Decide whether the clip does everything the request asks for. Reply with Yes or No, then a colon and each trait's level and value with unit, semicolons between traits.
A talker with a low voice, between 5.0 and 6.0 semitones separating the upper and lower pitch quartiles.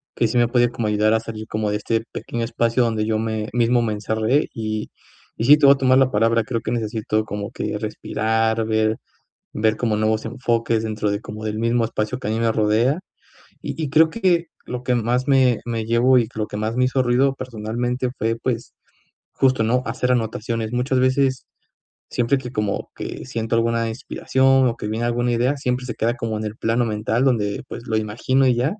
No: low, 115 Hz; narrow, 2.5 semitones